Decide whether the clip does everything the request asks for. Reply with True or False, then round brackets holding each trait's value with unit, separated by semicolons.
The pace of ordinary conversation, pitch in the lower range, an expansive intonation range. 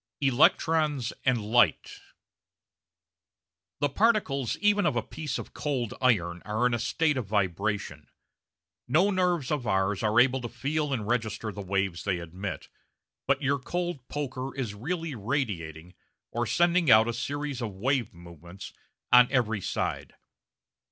True (145 wpm; 125 Hz; 5.9 semitones)